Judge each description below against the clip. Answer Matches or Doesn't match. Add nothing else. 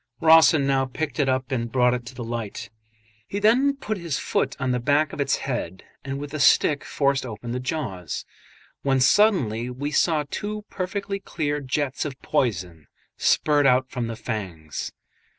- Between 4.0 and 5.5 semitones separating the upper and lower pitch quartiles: Matches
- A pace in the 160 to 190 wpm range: Matches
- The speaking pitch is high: Doesn't match